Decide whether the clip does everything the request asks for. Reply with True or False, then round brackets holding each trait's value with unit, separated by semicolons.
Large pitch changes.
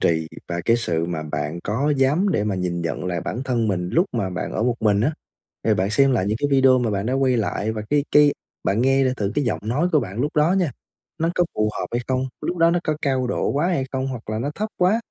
True (5.9 semitones)